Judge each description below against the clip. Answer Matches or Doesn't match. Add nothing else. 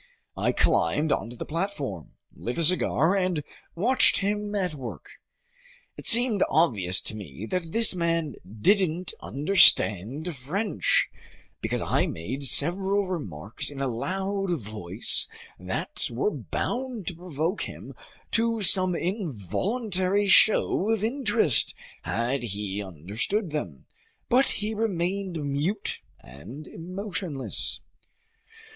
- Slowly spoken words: Matches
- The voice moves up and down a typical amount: Doesn't match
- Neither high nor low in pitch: Matches